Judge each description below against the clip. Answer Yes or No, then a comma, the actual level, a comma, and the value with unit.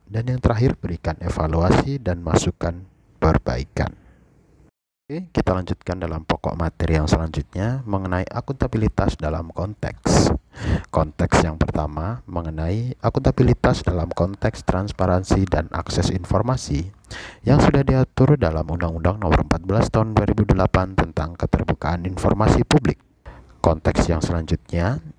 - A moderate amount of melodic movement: Yes, average, 4.9 semitones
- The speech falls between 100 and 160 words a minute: Yes, fast, 110 wpm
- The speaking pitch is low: Yes, very low, 90 Hz